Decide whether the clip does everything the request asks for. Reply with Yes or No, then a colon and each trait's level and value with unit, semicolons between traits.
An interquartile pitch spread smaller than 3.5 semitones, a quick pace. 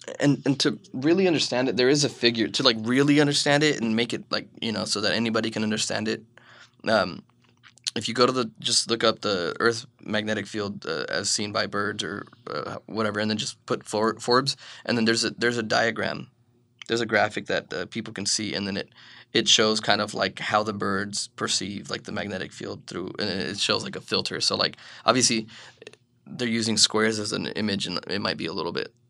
Yes: narrow, 2.4 semitones; fast, 225 wpm